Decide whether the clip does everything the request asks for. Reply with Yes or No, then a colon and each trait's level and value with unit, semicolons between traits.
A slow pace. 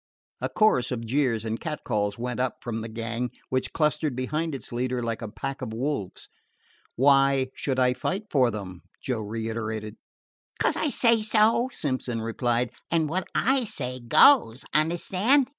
No: average, 160 wpm